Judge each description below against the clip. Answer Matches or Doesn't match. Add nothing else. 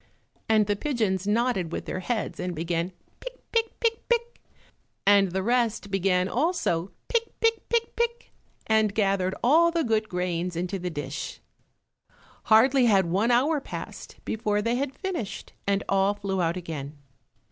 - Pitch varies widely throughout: Matches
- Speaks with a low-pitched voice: Doesn't match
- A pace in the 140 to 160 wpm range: Matches